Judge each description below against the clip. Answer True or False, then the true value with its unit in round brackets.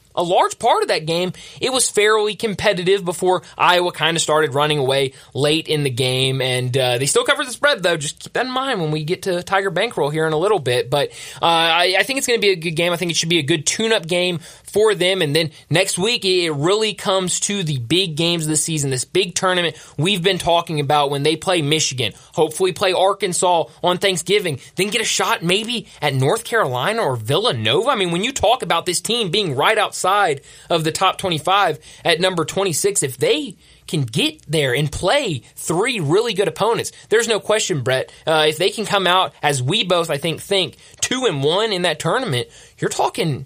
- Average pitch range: True (4.2 semitones)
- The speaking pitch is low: False (175 Hz)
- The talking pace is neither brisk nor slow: False (225 wpm)